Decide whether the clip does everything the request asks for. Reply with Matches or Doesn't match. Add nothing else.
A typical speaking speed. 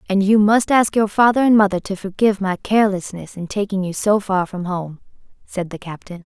Doesn't match